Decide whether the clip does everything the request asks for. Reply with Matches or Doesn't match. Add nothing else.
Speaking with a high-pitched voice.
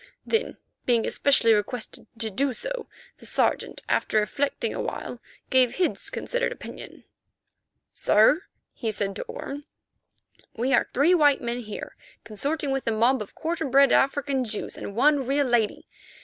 Matches